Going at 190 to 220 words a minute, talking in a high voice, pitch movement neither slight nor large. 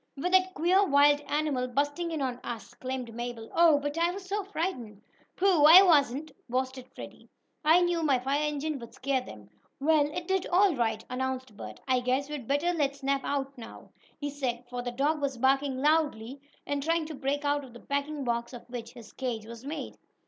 Yes: average, 200 wpm; very high, 280 Hz; average, 3.6 semitones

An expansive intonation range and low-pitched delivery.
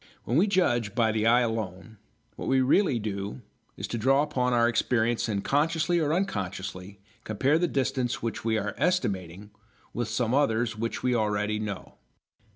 No: average, 4.3 semitones; low, 115 Hz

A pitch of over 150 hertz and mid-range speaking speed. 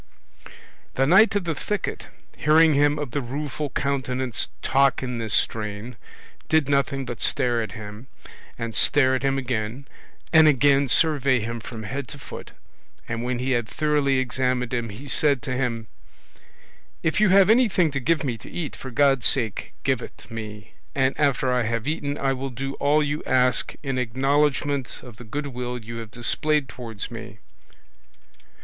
No: low, 130 Hz; average, 170 wpm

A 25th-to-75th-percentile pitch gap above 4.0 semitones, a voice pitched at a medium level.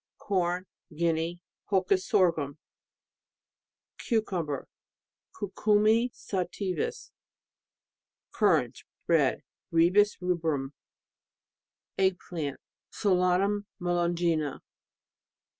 No: average, 3.0 semitones; medium, 180 Hz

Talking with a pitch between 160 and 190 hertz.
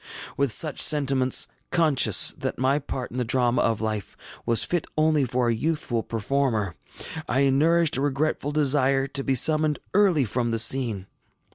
No: low, 135 Hz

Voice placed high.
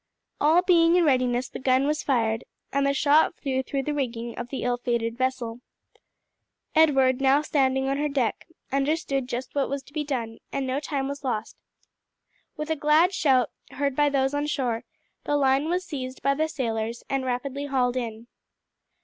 Yes: very high, 270 Hz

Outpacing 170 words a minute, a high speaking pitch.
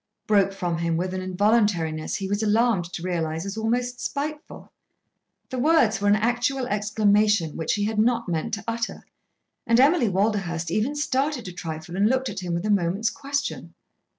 Yes: average, 180 wpm; high, 210 Hz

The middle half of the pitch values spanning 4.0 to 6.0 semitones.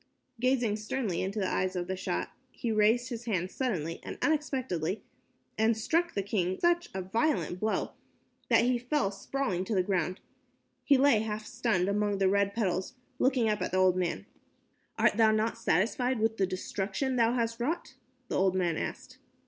Yes: average, 4.6 semitones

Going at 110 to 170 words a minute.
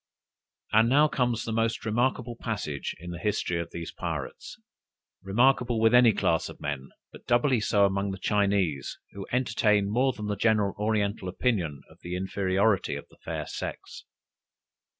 Yes: average, 160 wpm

